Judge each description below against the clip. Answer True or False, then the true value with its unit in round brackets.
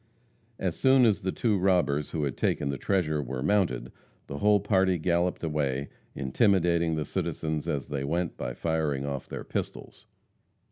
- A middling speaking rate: True (160 wpm)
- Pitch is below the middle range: True (80 Hz)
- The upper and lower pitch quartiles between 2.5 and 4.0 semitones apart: False (4.9 semitones)